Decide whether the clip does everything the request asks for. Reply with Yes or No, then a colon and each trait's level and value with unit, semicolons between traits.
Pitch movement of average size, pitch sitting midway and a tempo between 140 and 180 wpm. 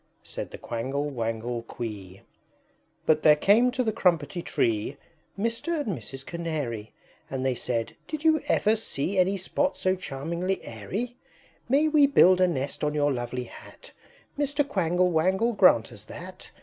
No: wide, 8.5 semitones; medium, 170 Hz; average, 160 wpm